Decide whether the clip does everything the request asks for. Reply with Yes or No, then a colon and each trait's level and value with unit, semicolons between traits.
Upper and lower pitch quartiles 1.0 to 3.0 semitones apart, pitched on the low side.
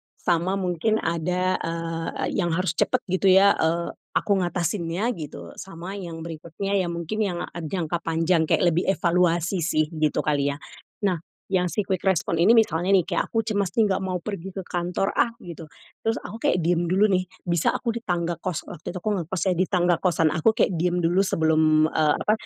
No: narrow, 2.6 semitones; medium, 175 Hz